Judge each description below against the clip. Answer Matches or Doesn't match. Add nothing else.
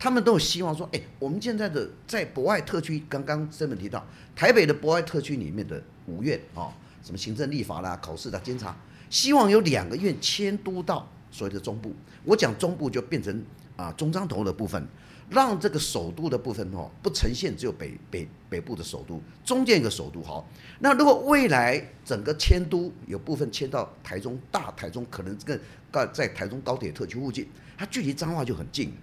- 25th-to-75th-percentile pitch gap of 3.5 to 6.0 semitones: Doesn't match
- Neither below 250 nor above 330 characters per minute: Matches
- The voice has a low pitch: Doesn't match